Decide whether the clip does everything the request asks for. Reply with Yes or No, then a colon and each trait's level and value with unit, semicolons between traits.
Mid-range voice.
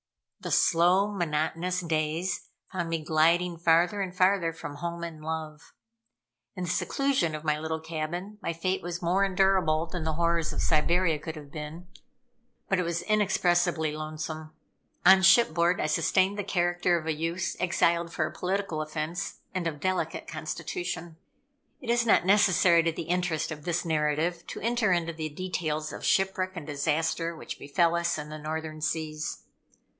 Yes: medium, 170 Hz